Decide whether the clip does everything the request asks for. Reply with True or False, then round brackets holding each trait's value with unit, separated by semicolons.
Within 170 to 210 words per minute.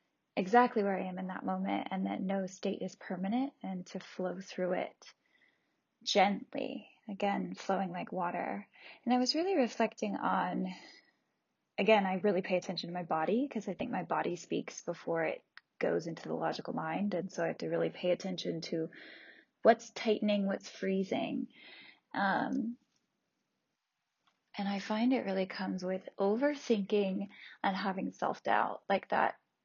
False (155 wpm)